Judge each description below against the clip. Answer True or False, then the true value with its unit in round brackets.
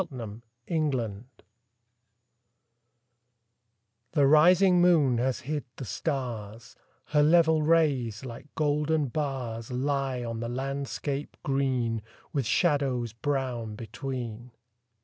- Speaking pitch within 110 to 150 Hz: True (135 Hz)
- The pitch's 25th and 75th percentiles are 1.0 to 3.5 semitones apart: False (4.0 semitones)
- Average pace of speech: False (90 wpm)